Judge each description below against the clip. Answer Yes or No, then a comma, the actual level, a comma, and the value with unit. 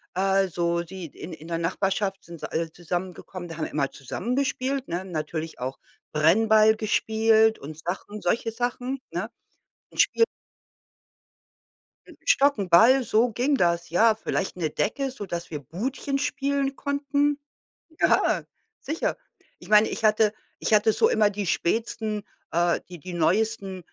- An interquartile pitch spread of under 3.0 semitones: No, wide, 5.4 semitones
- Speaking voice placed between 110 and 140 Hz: No, high, 205 Hz